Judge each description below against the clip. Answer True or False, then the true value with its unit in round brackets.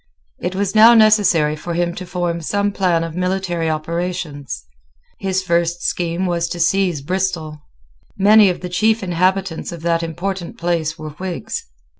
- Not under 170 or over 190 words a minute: False (155 wpm)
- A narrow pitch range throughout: True (2.3 semitones)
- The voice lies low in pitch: False (175 Hz)